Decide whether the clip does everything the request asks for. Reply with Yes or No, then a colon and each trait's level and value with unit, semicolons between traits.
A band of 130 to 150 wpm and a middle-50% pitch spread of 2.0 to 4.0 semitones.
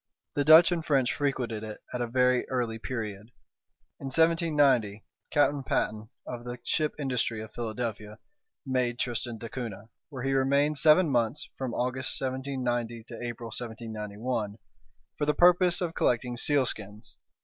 Yes: average, 140 wpm; average, 3.6 semitones